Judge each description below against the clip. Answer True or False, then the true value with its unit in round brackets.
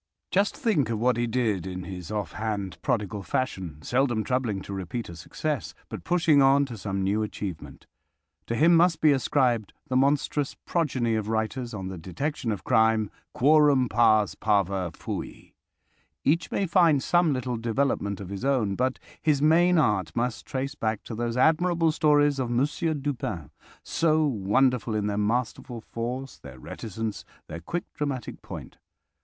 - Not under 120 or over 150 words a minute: False (160 wpm)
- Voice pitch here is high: False (120 Hz)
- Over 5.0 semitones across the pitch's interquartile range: True (5.5 semitones)